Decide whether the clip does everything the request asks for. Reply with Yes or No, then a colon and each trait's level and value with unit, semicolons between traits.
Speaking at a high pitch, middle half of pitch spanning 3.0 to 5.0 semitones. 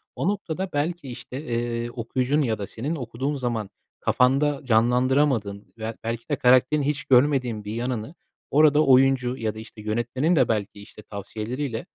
No: low, 125 Hz; average, 4.0 semitones